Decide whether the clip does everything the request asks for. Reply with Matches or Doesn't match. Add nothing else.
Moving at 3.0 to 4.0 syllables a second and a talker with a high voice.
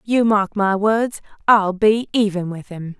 Matches